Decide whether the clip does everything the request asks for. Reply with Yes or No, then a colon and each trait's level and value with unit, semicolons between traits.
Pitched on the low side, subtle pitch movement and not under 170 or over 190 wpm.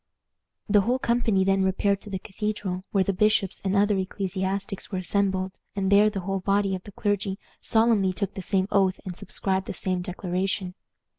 No: high, 195 Hz; narrow, 1.4 semitones; average, 180 wpm